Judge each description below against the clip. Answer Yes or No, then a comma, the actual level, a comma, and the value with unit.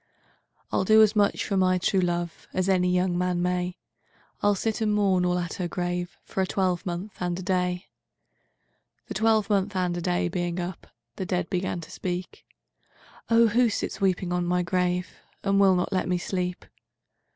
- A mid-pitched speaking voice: Yes, medium, 180 Hz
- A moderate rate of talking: Yes, average, 155 wpm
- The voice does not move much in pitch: Yes, narrow, 1.6 semitones